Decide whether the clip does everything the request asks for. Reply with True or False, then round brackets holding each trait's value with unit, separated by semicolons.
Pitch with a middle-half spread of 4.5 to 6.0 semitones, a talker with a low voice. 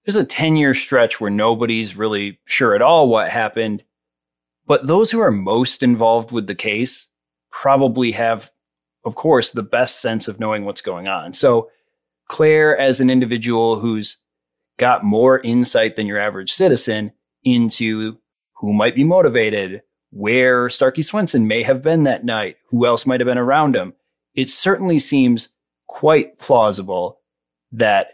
False (3.7 semitones; 115 Hz)